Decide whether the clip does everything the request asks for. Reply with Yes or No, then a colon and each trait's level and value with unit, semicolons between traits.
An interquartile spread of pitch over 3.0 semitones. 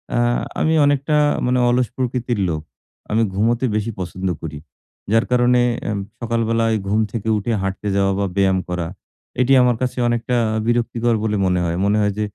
Yes: average, 3.6 semitones